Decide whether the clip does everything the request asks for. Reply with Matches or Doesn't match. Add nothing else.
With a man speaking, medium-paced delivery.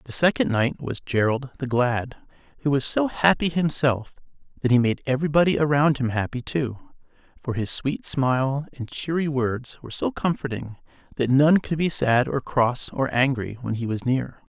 Matches